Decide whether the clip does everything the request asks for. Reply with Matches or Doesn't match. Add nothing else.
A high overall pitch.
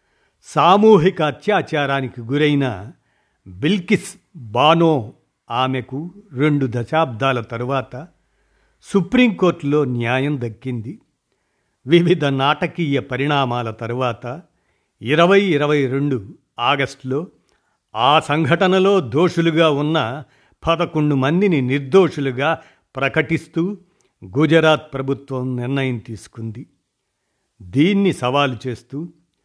Doesn't match